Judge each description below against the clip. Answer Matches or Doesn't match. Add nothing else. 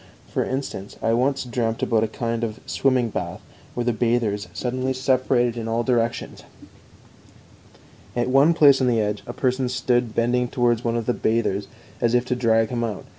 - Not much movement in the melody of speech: Matches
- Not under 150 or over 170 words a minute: Doesn't match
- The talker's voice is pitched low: Matches